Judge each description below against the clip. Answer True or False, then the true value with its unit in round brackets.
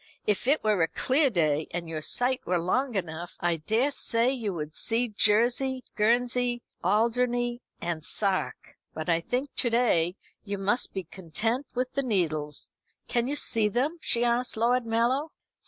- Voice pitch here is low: False (230 Hz)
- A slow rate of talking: False (160 wpm)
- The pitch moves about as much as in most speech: False (5.9 semitones)